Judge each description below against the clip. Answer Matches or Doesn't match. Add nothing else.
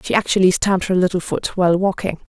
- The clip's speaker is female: Matches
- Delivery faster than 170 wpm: Matches